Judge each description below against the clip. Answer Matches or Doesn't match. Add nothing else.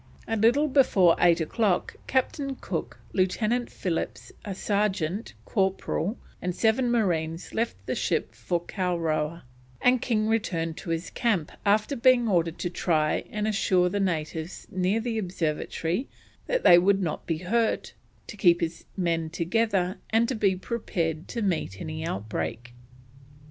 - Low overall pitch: Doesn't match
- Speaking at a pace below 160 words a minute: Matches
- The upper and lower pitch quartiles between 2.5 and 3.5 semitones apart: Doesn't match